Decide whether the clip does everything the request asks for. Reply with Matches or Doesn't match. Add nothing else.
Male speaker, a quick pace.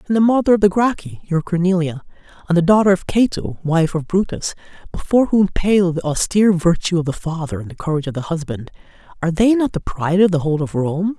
Doesn't match